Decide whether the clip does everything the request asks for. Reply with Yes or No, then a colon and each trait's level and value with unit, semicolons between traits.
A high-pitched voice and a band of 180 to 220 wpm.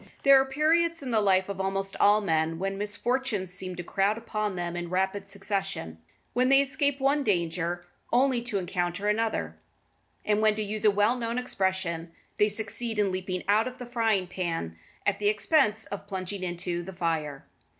Yes: high, 200 Hz; average, 190 wpm